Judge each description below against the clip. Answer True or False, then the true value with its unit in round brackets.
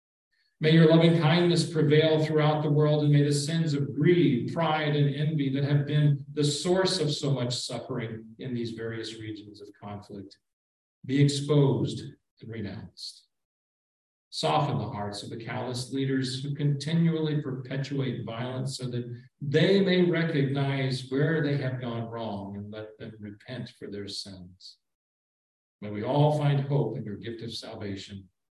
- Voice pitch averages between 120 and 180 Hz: True (135 Hz)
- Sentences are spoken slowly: False (155 wpm)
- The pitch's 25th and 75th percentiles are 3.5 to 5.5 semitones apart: True (5.0 semitones)